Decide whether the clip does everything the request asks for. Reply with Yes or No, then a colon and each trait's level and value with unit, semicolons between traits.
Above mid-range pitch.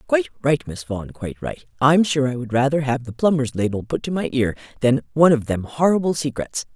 No: low, 135 Hz